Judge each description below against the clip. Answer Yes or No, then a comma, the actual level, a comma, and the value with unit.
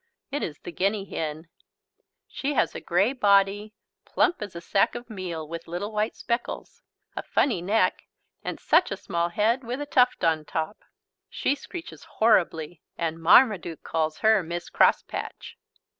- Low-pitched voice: No, high, 195 Hz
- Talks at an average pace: Yes, average, 160 wpm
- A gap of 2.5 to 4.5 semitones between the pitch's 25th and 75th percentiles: No, average, 5.2 semitones